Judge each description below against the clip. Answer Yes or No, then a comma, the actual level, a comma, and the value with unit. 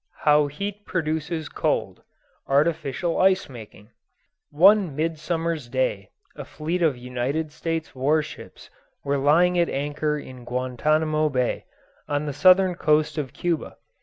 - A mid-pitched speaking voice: Yes, medium, 155 Hz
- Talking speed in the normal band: No, slow, 130 wpm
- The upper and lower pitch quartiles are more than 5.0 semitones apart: No, average, 3.4 semitones